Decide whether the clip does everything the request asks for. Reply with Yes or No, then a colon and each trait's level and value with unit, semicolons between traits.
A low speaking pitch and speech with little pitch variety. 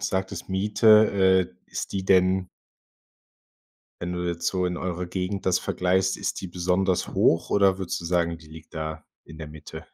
Yes: very low, 90 Hz; narrow, 1.7 semitones